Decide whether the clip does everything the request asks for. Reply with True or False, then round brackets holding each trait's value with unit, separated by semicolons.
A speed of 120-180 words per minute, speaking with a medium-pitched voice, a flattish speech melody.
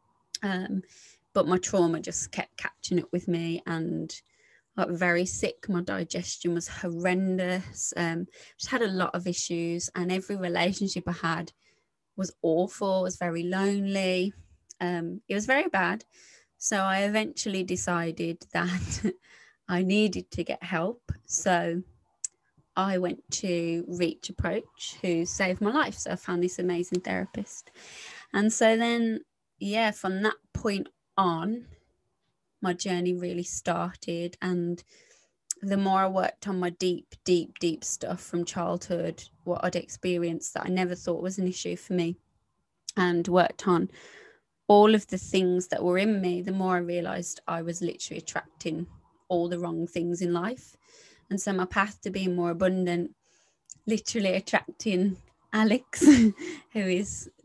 True (150 wpm; 180 Hz; 2.2 semitones)